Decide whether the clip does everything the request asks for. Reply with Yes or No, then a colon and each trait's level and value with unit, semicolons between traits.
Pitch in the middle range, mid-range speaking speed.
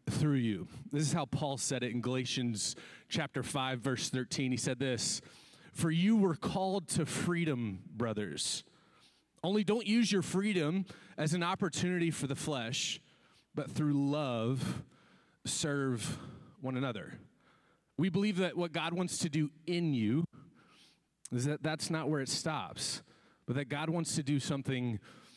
Yes: medium, 150 Hz; average, 155 wpm